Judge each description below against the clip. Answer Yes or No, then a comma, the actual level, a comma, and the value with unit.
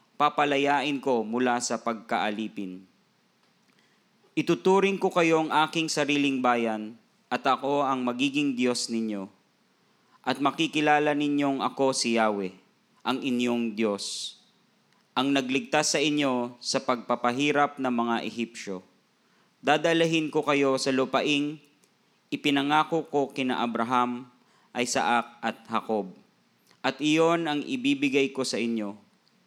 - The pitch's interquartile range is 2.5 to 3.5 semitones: No, average, 3.9 semitones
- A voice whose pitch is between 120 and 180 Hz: Yes, low, 135 Hz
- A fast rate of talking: No, slow, 110 wpm